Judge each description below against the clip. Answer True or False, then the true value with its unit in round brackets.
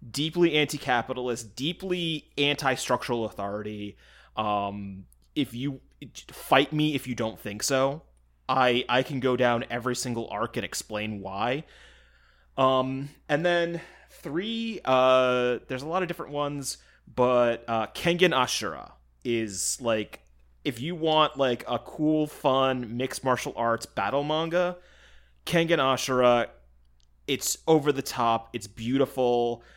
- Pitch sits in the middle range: False (125 Hz)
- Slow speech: True (125 wpm)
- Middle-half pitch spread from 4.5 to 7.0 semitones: True (4.9 semitones)